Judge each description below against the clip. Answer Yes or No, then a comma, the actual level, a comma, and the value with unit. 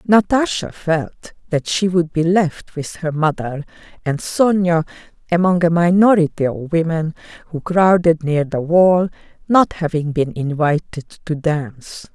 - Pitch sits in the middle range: Yes, medium, 165 Hz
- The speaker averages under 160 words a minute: Yes, average, 140 wpm